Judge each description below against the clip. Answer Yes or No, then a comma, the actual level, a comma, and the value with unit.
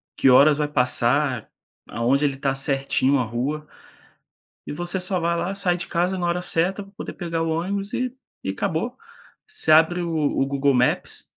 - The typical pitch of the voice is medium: Yes, medium, 160 Hz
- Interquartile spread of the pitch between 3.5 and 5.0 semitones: Yes, average, 4.5 semitones